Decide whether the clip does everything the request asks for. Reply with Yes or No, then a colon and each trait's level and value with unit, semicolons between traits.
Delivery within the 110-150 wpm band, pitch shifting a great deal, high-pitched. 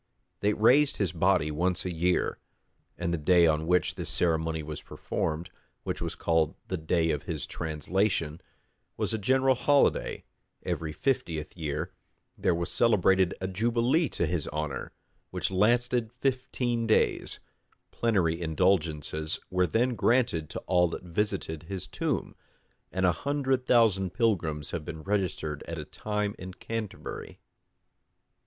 No: average, 140 wpm; wide, 5.8 semitones; very low, 90 Hz